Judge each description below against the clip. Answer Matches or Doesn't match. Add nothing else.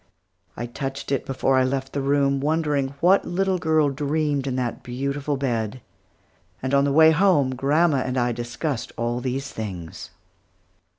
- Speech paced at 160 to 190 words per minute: Matches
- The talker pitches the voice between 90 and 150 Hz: Matches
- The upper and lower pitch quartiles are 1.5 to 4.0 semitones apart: Matches